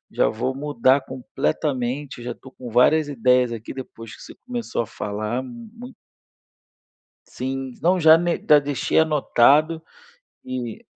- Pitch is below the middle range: Yes, low, 130 Hz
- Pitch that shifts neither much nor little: Yes, average, 4.1 semitones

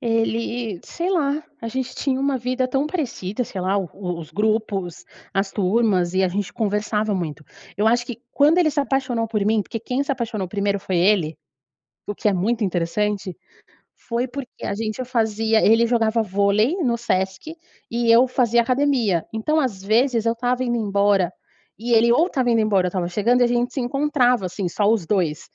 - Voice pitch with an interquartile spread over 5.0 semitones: No, average, 3.8 semitones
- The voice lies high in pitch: Yes, high, 225 Hz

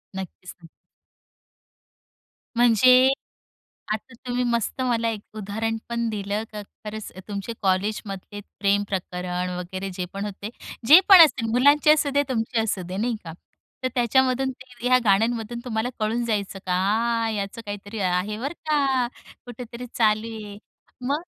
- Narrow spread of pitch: No, average, 3.5 semitones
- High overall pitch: Yes, high, 220 Hz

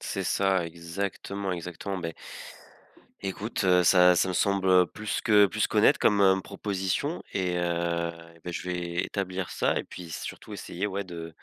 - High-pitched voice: No, very low, 90 Hz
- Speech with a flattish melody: Yes, narrow, 2.2 semitones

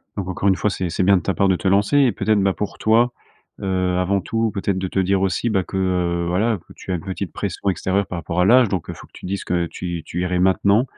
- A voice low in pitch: Yes, very low, 95 Hz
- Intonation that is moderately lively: No, narrow, 1.9 semitones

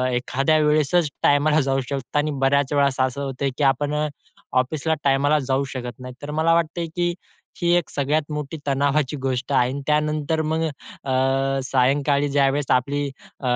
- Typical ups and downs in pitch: No, narrow, 2.1 semitones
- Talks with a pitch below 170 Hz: Yes, medium, 140 Hz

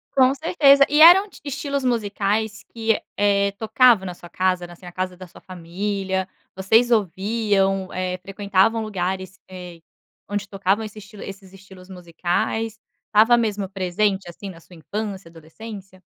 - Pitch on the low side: No, high, 195 Hz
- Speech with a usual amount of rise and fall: Yes, average, 3.0 semitones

